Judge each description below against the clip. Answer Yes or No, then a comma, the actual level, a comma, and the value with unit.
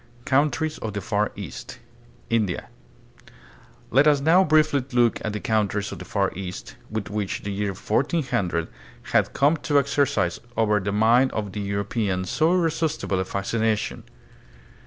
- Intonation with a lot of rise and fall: Yes, wide, 5.9 semitones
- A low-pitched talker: Yes, low, 110 Hz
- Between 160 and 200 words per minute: No, average, 150 wpm